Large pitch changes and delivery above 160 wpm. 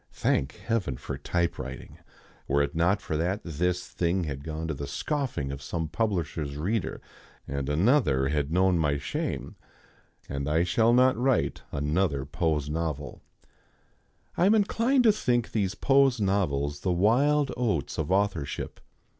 No: wide, 7.5 semitones; average, 145 wpm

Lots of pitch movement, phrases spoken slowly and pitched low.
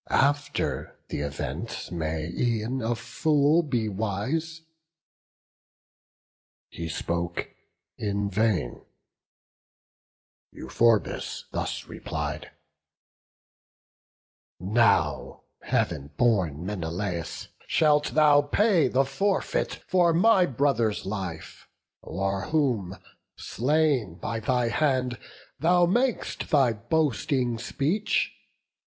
Yes: wide, 7.6 semitones; slow, 85 wpm; low, 120 Hz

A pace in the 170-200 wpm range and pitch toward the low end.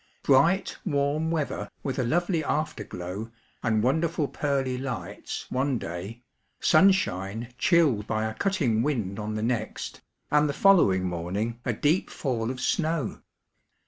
No: average, 140 wpm; low, 130 Hz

